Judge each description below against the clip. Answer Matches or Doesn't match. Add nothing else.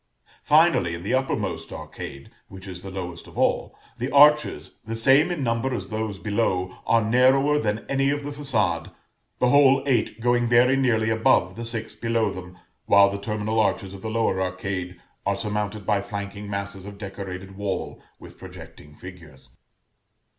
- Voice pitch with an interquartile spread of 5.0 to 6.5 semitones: Doesn't match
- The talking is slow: Doesn't match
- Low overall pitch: Matches